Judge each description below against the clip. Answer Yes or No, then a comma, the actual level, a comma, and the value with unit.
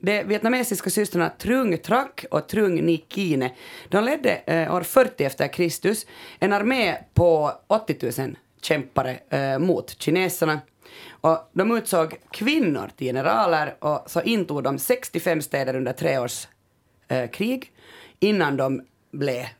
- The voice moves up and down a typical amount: No, wide, 6.8 semitones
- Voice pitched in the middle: Yes, medium, 170 Hz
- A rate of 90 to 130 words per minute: Yes, slow, 125 wpm